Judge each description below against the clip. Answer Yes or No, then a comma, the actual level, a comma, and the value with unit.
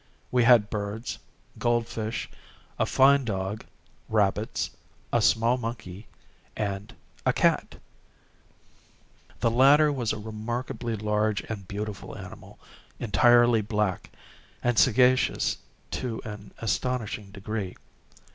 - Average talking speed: No, slow, 105 wpm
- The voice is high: No, low, 110 Hz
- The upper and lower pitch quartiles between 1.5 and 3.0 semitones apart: Yes, narrow, 2.6 semitones